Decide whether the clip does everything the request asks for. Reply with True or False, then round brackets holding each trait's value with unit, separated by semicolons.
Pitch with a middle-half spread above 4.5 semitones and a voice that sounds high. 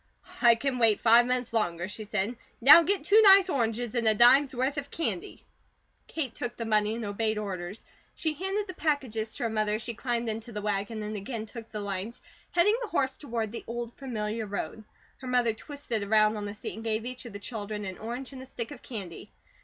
False (3.5 semitones; 230 Hz)